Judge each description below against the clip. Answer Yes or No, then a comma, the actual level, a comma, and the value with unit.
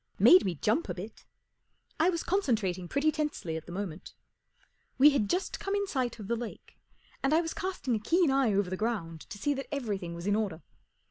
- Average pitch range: No, wide, 7.8 semitones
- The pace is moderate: No, fast, 210 wpm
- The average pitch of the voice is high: Yes, high, 230 Hz